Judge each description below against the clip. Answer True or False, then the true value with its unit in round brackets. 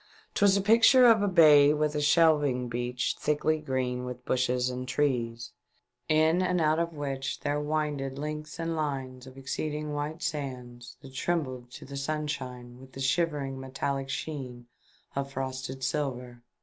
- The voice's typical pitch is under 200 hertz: True (140 Hz)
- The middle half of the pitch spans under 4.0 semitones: True (3.0 semitones)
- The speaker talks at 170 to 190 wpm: False (155 wpm)